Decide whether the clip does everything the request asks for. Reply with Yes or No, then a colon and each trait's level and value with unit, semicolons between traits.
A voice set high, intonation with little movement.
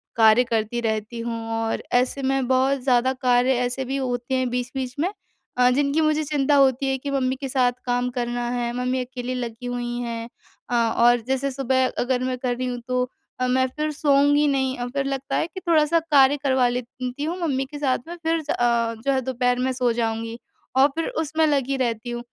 Yes: very high, 255 Hz; narrow, 2.1 semitones